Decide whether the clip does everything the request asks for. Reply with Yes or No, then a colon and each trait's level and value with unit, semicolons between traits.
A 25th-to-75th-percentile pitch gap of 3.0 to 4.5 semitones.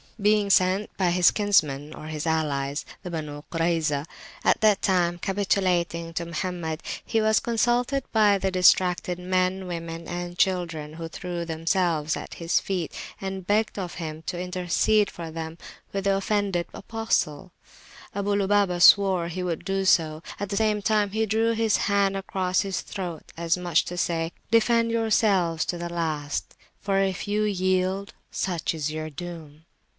Yes: average, 3.3 semitones